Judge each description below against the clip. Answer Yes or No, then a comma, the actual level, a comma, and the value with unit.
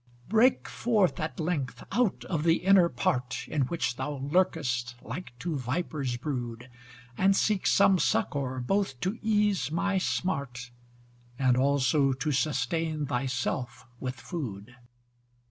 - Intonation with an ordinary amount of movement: No, wide, 6.1 semitones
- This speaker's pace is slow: Yes, slow, 130 wpm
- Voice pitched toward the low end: No, medium, 145 Hz